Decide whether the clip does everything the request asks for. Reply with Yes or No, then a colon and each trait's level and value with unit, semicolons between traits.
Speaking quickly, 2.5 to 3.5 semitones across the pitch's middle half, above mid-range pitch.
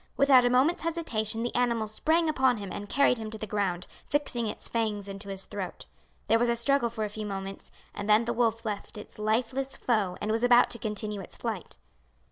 Yes: fast, 215 wpm; average, 2.9 semitones; high, 225 Hz